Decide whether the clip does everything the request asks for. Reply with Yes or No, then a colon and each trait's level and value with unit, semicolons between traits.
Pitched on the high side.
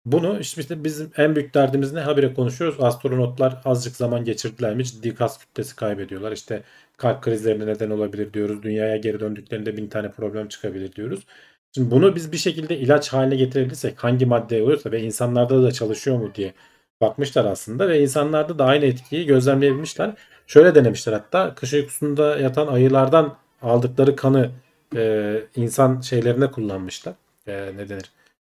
No: low, 125 Hz